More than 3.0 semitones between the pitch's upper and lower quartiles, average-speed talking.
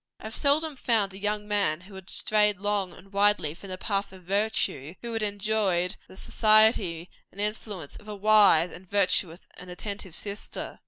No: narrow, 2.5 semitones; average, 180 wpm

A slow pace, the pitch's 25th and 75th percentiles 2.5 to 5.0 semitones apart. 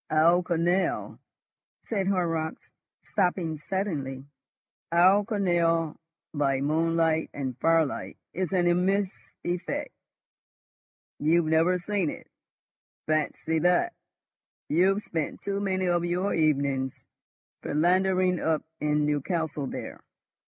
Yes: slow, 100 wpm; average, 3.0 semitones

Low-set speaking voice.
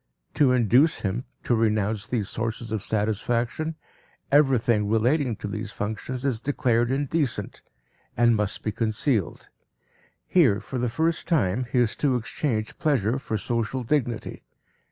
Yes: low, 120 Hz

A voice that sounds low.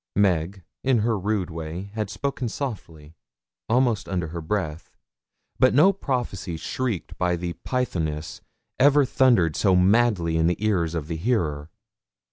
Yes: very low, 95 Hz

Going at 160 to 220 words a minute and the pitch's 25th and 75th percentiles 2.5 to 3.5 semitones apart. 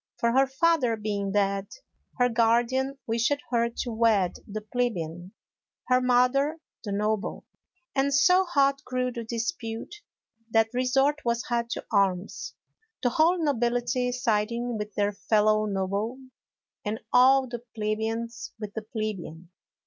No: slow, 135 wpm; average, 3.1 semitones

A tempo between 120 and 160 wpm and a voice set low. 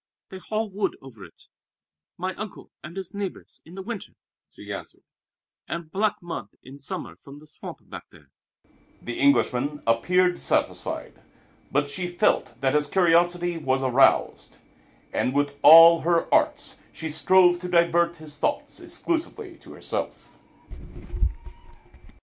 No: average, 140 wpm; medium, 170 Hz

